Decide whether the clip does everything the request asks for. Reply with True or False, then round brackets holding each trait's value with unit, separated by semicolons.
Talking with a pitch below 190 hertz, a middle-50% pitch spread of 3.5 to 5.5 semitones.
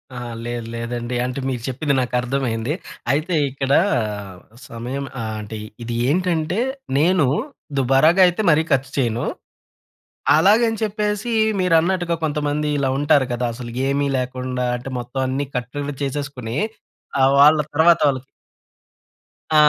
True (140 Hz; 4.1 semitones)